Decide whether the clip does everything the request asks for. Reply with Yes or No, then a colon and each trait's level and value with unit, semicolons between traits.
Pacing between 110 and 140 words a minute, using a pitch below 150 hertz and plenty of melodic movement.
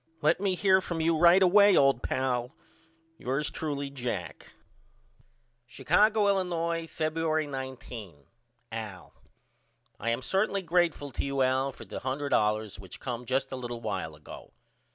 Yes: slow, 135 wpm; medium, 140 Hz; wide, 5.7 semitones